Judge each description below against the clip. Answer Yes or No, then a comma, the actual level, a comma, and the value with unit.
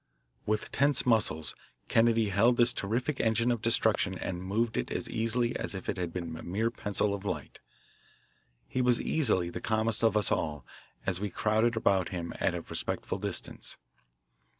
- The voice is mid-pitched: No, low, 110 Hz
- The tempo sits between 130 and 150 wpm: No, average, 175 wpm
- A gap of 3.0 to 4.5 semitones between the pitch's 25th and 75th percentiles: Yes, average, 3.7 semitones